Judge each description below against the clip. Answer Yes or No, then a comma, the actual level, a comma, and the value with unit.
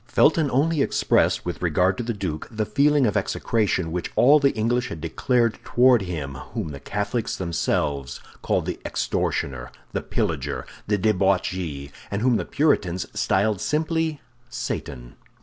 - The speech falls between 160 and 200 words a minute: No, average, 150 wpm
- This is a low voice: Yes, low, 105 Hz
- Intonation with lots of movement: Yes, wide, 6.7 semitones